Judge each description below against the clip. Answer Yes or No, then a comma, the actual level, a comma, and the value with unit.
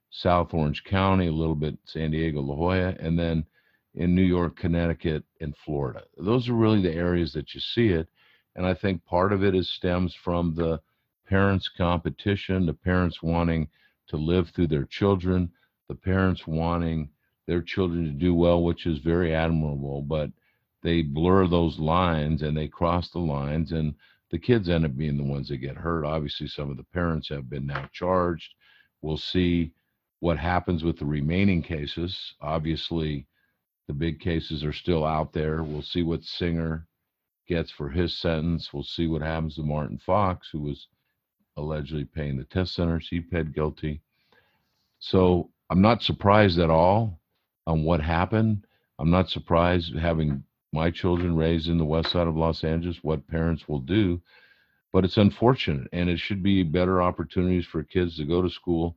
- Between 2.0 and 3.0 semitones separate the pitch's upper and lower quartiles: Yes, narrow, 2.4 semitones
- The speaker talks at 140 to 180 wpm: Yes, average, 175 wpm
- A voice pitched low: Yes, very low, 85 Hz